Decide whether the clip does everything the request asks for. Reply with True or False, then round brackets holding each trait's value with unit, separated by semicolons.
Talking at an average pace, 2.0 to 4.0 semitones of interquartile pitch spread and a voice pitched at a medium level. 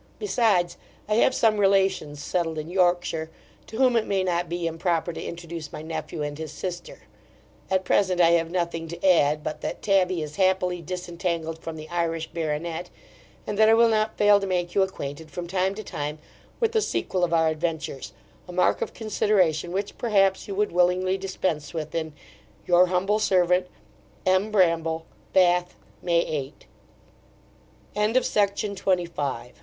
True (175 wpm; 2.9 semitones; 175 Hz)